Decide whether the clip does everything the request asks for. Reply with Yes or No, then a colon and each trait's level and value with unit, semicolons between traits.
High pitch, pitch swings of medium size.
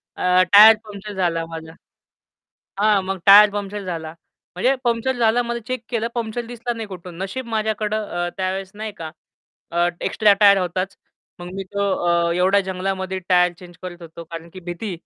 Yes: high, 195 Hz; average, 3.4 semitones